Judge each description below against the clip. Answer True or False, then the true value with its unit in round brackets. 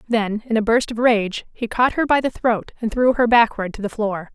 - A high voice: True (225 Hz)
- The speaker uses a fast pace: True (265 wpm)